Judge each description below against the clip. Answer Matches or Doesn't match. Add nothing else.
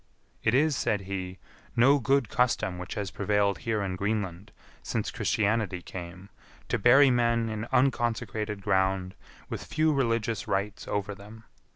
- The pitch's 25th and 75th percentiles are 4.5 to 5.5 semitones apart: Doesn't match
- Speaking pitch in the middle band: Doesn't match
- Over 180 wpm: Doesn't match